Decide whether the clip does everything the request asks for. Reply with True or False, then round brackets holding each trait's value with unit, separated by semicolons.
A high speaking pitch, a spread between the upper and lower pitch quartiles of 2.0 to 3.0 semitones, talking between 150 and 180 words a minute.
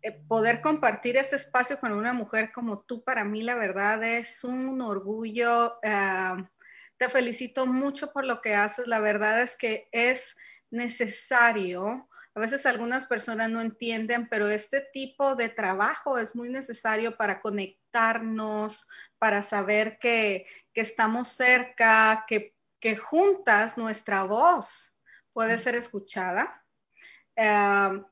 False (230 Hz; 2.7 semitones; 130 wpm)